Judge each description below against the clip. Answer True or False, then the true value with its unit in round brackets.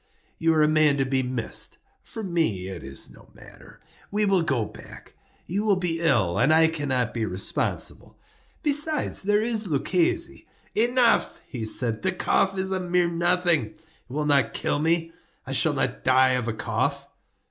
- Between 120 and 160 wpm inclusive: False (175 wpm)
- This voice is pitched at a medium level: True (160 Hz)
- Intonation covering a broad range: True (6.5 semitones)